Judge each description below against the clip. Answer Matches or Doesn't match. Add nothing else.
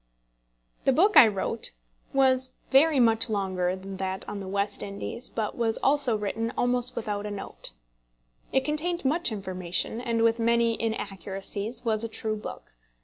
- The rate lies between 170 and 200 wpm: Doesn't match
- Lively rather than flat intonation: Doesn't match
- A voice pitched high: Matches